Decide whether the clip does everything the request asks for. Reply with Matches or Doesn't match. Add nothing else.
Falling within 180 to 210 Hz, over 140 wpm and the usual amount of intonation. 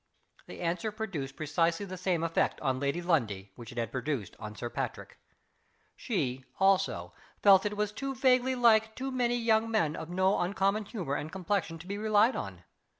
Doesn't match